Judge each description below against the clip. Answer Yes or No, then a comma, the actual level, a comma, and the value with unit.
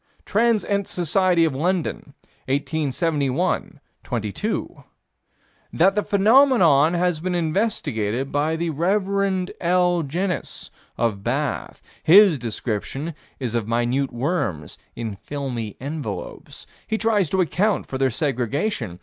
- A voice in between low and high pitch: Yes, medium, 155 Hz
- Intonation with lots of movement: Yes, wide, 6.4 semitones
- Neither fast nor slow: No, slow, 115 wpm